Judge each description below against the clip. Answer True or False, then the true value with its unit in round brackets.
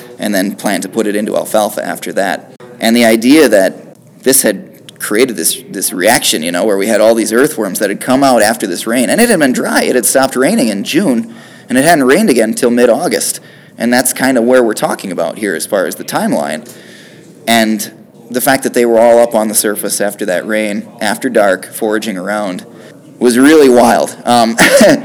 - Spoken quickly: True (215 wpm)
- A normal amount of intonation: False (2.3 semitones)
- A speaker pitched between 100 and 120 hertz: True (115 Hz)